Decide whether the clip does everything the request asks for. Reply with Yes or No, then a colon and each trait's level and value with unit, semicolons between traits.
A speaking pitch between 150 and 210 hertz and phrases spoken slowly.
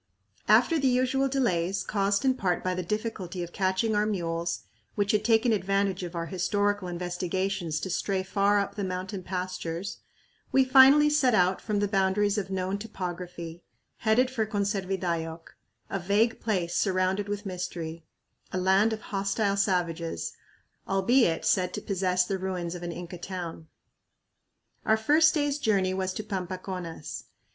No: high, 190 Hz; average, 150 wpm